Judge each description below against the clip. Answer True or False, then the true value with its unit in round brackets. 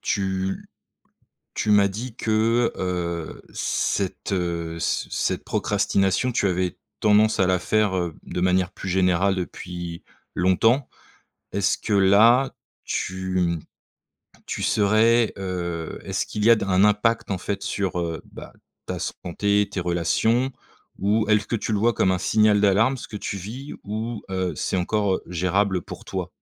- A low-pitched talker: True (100 Hz)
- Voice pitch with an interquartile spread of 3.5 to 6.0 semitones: False (2.9 semitones)